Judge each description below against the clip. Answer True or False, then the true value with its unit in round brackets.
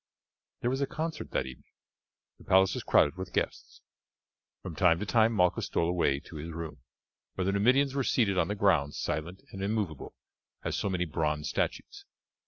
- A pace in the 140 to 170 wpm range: False (185 wpm)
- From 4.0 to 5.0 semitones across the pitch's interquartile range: True (4.7 semitones)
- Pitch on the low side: True (90 Hz)